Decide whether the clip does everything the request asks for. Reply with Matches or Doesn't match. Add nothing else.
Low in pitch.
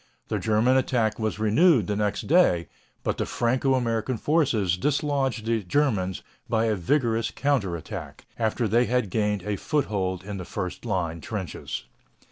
Matches